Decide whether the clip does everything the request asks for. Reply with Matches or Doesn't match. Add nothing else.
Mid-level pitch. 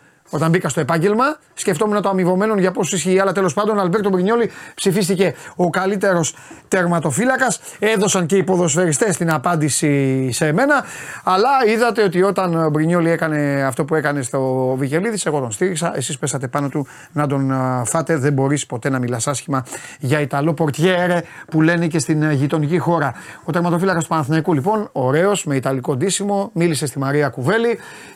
Matches